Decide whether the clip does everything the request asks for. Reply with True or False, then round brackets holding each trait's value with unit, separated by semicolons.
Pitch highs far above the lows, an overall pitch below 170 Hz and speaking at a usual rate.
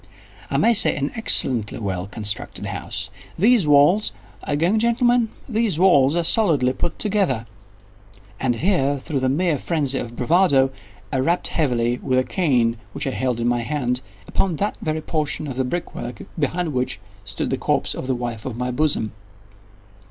True (5.8 semitones; 140 Hz; 170 wpm)